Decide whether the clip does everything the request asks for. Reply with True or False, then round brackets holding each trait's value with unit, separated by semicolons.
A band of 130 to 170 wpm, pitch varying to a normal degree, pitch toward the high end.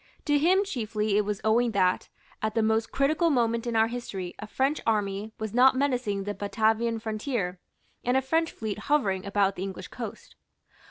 False (180 wpm; 3.6 semitones; 220 Hz)